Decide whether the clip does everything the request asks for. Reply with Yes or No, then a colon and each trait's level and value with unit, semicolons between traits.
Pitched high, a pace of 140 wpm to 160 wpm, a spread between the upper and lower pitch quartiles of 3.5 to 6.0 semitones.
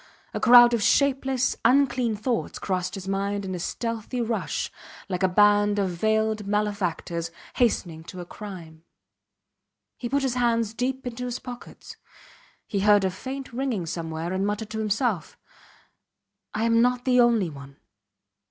Yes: high, 215 Hz; average, 150 wpm; average, 4.4 semitones